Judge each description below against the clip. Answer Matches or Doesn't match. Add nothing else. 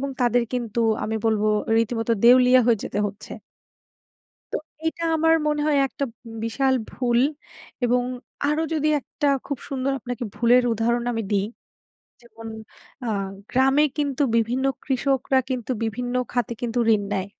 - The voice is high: Matches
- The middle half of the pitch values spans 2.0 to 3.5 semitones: Matches